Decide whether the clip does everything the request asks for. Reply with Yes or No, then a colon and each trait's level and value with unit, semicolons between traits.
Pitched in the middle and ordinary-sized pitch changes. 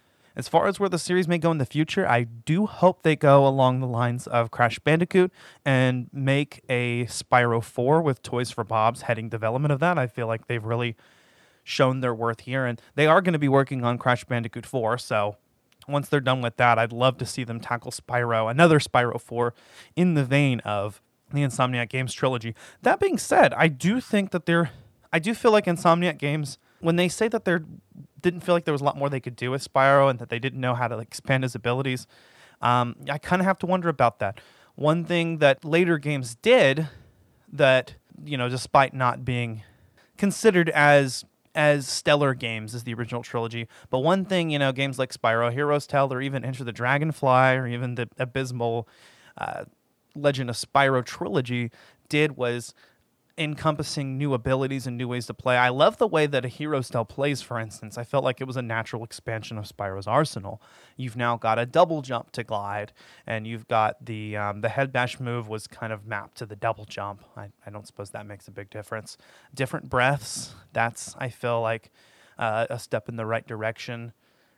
No: low, 125 Hz; average, 3.8 semitones